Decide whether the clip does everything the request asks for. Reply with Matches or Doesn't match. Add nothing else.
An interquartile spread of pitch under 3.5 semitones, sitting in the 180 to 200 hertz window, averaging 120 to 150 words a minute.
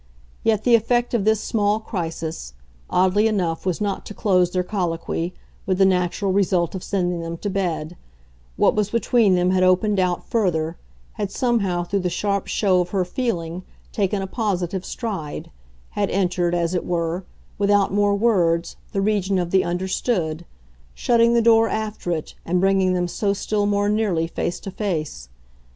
Doesn't match